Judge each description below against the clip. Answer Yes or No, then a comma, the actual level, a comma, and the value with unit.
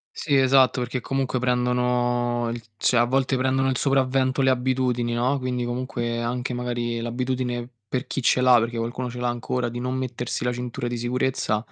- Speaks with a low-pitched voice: Yes, low, 125 Hz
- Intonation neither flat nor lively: No, narrow, 1.2 semitones